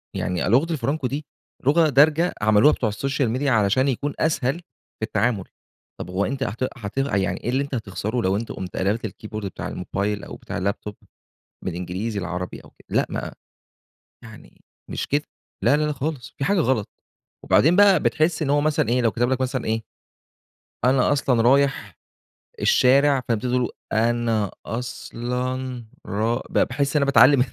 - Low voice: Yes, low, 125 Hz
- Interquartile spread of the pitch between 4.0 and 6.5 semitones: Yes, average, 4.6 semitones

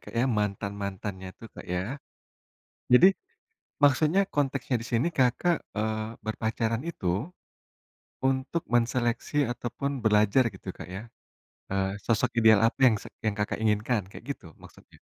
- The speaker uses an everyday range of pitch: Yes, average, 3.7 semitones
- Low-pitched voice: Yes, low, 115 Hz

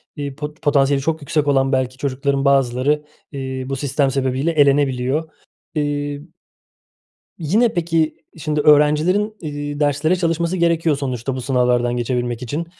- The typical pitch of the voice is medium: Yes, medium, 145 Hz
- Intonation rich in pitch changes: No, average, 2.7 semitones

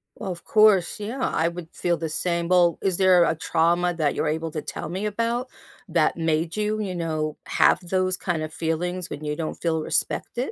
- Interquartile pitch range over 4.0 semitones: No, average, 2.7 semitones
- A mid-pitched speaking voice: Yes, medium, 175 Hz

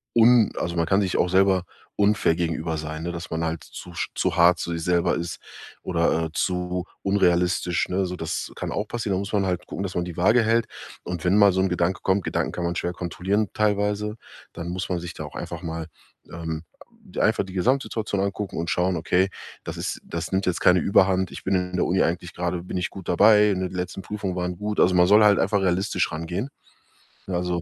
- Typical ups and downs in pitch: No, narrow, 2.3 semitones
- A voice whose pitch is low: Yes, very low, 90 Hz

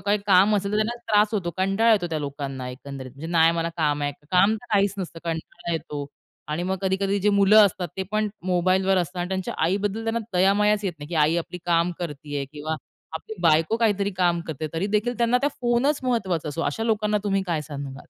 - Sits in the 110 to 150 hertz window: No, medium, 185 Hz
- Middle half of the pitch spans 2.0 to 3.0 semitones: No, average, 4.4 semitones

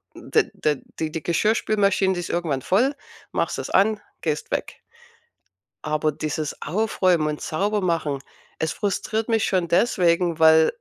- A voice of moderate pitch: Yes, medium, 170 Hz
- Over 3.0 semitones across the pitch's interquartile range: Yes, average, 4.5 semitones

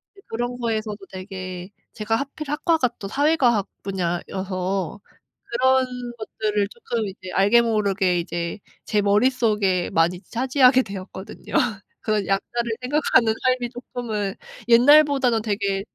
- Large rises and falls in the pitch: No, average, 4.3 semitones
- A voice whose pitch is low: No, high, 215 Hz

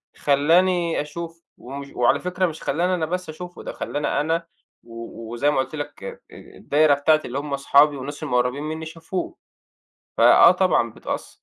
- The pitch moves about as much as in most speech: Yes, average, 3.3 semitones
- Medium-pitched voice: Yes, medium, 150 Hz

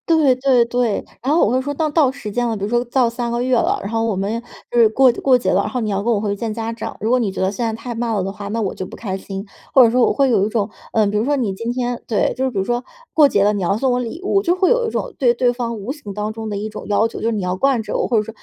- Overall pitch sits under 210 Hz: No, high, 230 Hz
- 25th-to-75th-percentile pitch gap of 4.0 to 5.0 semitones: No, average, 3.4 semitones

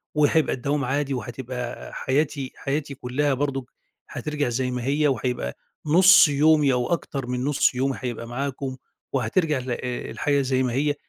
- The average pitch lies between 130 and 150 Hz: Yes, low, 135 Hz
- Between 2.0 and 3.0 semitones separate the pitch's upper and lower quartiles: Yes, narrow, 2.6 semitones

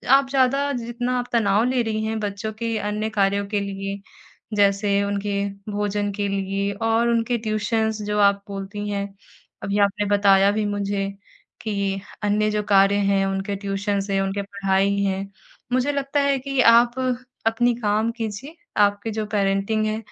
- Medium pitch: No, high, 205 Hz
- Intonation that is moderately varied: No, narrow, 2.1 semitones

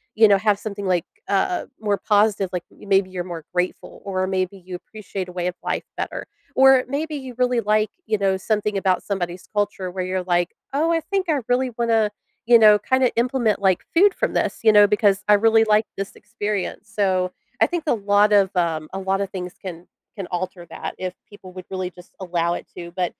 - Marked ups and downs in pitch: No, average, 3.1 semitones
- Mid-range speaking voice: No, high, 200 Hz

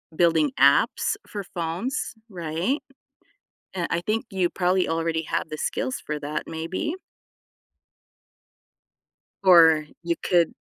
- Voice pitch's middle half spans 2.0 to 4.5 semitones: Yes, average, 2.8 semitones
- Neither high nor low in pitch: Yes, medium, 170 Hz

